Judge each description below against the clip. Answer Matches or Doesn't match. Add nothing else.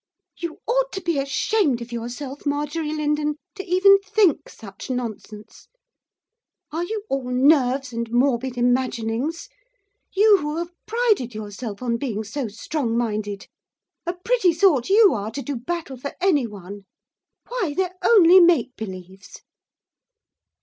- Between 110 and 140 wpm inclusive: Matches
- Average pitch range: Doesn't match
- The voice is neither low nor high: Doesn't match